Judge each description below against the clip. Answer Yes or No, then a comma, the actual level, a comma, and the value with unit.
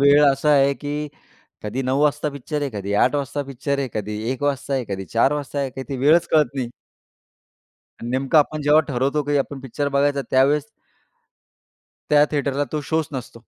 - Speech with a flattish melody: Yes, narrow, 1.9 semitones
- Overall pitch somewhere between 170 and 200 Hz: No, medium, 140 Hz